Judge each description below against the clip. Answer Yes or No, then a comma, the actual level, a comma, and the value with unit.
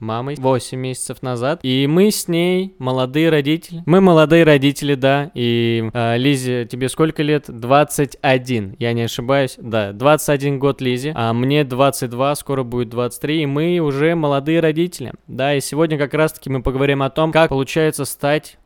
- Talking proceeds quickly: Yes, fast, 165 wpm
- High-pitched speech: No, medium, 140 Hz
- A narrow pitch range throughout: No, average, 3.3 semitones